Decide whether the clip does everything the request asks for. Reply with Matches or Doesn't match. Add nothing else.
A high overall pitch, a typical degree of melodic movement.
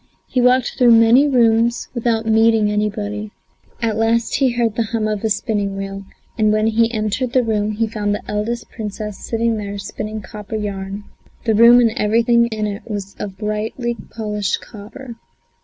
Doesn't match